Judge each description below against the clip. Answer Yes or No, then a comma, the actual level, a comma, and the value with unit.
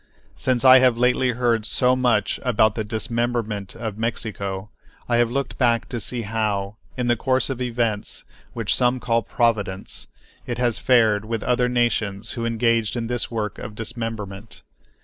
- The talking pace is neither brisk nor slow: Yes, average, 165 wpm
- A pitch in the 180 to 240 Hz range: No, low, 115 Hz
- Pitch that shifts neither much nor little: No, narrow, 2.2 semitones